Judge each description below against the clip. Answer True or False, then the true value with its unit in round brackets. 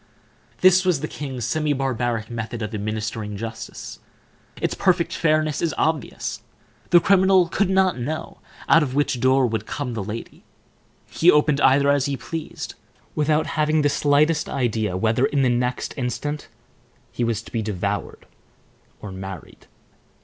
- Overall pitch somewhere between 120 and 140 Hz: True (135 Hz)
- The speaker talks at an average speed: True (150 wpm)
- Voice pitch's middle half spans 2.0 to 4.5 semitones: False (5.3 semitones)